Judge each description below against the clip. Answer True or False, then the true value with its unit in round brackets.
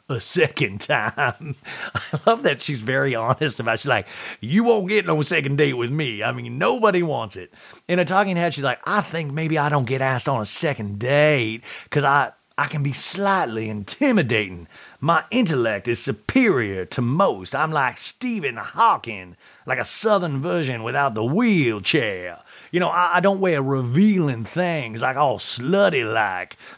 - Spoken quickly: False (175 wpm)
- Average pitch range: False (6.2 semitones)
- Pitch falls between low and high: True (145 Hz)